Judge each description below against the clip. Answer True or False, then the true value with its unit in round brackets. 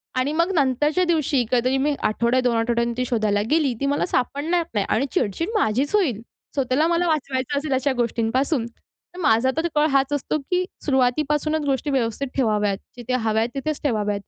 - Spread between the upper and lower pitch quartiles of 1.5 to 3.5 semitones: False (4.1 semitones)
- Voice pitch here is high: True (265 Hz)